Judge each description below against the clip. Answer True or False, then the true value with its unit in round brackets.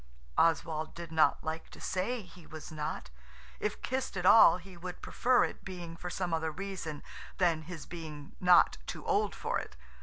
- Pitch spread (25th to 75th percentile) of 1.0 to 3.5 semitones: True (2.5 semitones)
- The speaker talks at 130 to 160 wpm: False (180 wpm)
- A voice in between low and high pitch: True (170 Hz)